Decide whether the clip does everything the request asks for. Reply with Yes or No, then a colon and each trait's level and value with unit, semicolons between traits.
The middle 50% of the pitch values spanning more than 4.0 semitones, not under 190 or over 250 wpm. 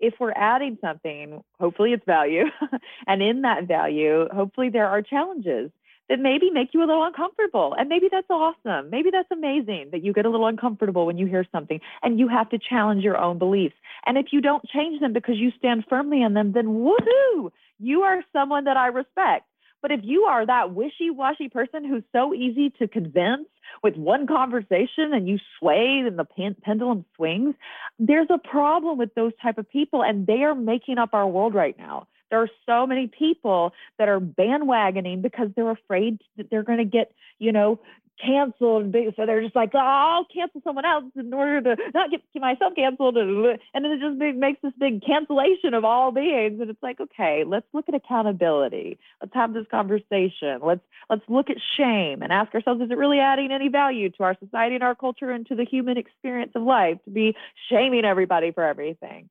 Yes: average, 5.1 semitones; average, 200 wpm